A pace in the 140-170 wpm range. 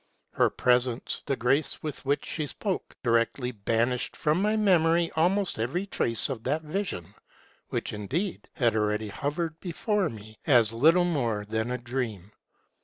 Yes: average, 155 wpm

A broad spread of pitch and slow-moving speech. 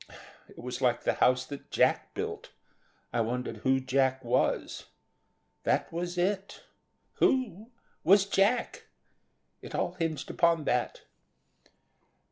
Yes: wide, 6.6 semitones; slow, 115 wpm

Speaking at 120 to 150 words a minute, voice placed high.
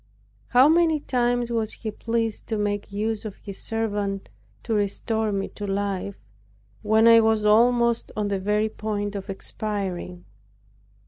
Yes: average, 145 wpm; high, 215 Hz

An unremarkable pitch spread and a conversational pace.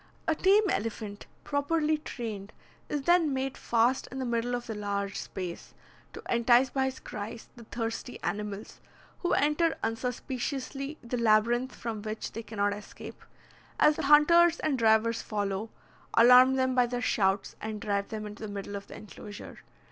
Yes: average, 4.0 semitones; average, 165 wpm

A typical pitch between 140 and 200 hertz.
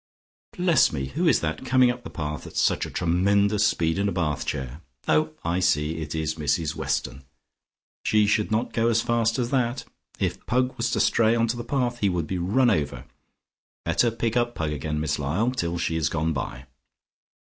No: low, 100 Hz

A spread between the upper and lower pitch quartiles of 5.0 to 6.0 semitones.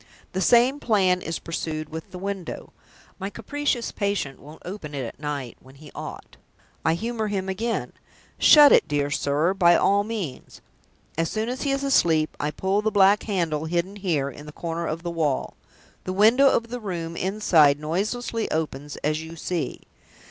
Yes: average, 5.3 semitones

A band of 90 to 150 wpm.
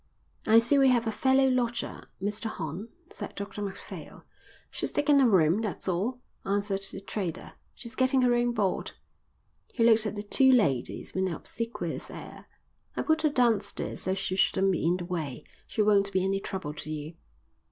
No: average, 185 wpm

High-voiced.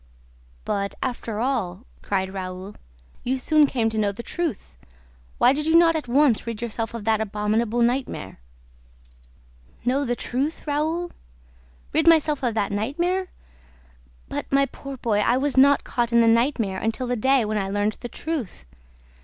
Yes: high, 240 Hz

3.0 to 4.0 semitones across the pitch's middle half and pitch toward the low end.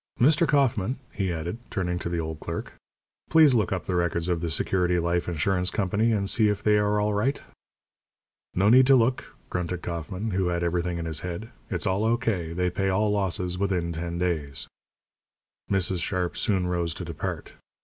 Yes: average, 3.3 semitones; very low, 90 Hz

